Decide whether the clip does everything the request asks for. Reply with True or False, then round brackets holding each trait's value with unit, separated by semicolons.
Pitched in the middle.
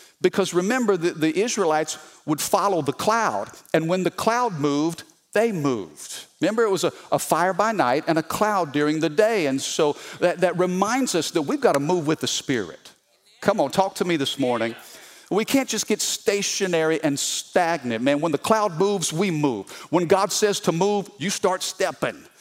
True (180 Hz)